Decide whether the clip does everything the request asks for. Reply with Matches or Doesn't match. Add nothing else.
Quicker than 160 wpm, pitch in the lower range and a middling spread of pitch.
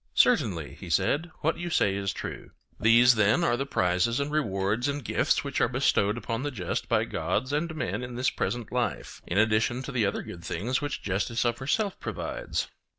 Doesn't match